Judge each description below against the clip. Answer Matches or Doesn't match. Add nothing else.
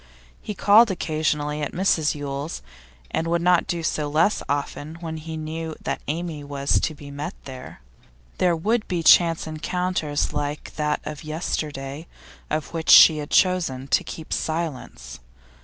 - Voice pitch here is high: Doesn't match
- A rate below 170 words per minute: Matches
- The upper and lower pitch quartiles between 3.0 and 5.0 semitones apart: Doesn't match